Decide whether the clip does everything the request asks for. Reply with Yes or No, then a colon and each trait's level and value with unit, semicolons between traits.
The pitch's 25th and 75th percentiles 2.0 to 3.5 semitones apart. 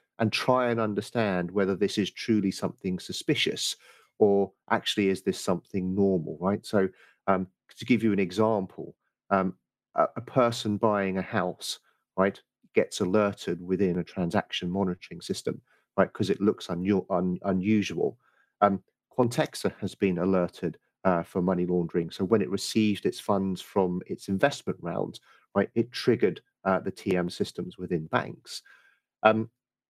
Yes: narrow, 2.5 semitones